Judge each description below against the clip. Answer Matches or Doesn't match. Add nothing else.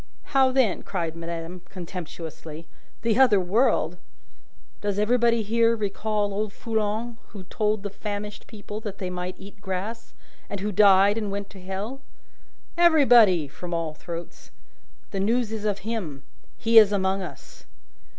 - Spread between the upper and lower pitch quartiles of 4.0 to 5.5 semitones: Doesn't match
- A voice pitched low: Doesn't match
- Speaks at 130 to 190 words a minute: Matches